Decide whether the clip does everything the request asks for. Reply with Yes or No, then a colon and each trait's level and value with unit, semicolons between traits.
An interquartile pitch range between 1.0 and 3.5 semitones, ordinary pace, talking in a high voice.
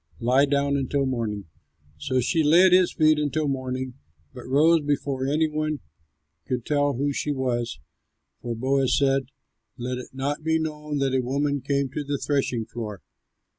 No: narrow, 2.5 semitones; average, 170 wpm; medium, 140 Hz